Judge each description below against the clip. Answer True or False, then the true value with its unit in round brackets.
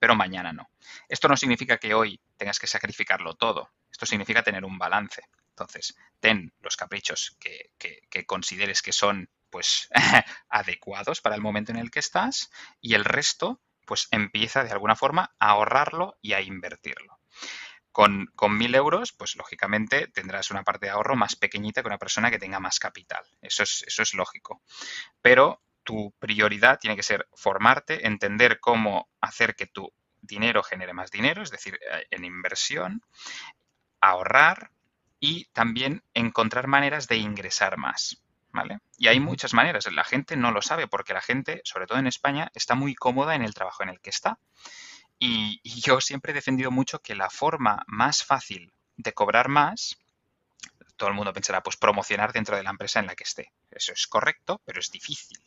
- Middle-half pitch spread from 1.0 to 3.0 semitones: False (4.4 semitones)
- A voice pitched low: True (115 Hz)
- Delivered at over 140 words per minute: True (175 wpm)